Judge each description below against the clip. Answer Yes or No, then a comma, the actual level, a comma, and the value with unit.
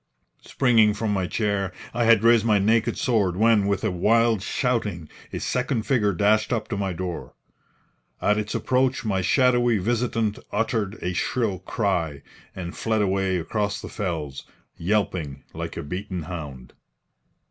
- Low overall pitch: Yes, low, 105 Hz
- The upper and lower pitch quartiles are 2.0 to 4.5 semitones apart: Yes, average, 3.8 semitones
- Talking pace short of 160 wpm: Yes, average, 150 wpm